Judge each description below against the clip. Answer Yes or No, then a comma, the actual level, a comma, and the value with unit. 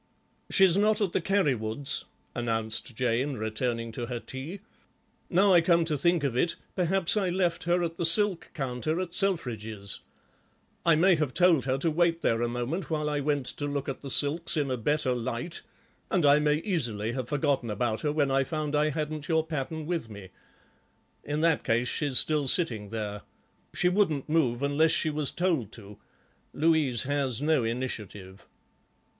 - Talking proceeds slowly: No, average, 175 wpm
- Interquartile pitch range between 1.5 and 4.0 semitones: No, average, 5.3 semitones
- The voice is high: No, medium, 145 Hz